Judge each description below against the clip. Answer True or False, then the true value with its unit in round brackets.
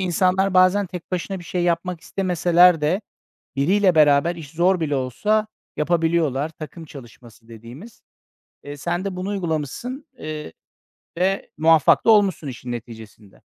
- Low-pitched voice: False (170 Hz)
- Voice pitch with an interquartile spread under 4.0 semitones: False (4.3 semitones)